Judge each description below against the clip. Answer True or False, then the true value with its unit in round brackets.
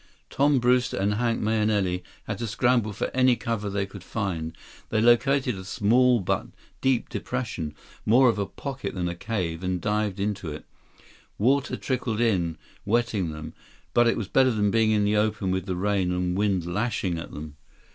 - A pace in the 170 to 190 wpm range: True (180 wpm)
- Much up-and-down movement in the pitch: False (4.3 semitones)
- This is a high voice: False (105 Hz)